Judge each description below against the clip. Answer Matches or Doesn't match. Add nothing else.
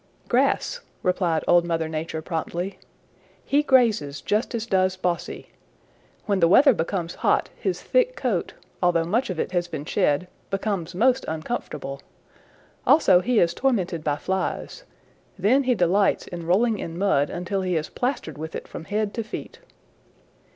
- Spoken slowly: Doesn't match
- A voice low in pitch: Doesn't match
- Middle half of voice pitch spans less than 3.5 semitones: Doesn't match